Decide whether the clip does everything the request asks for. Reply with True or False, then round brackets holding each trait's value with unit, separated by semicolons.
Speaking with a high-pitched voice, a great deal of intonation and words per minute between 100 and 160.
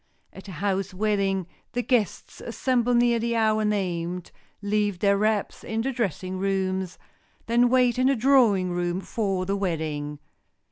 False (200 Hz; 3.9 semitones; 150 wpm)